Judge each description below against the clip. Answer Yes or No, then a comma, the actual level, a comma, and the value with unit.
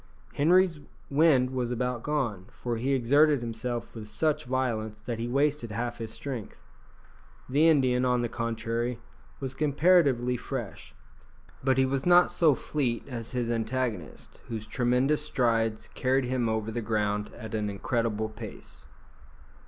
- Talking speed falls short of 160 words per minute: Yes, average, 145 wpm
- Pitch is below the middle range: Yes, low, 120 Hz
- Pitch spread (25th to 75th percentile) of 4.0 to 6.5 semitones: No, average, 3.1 semitones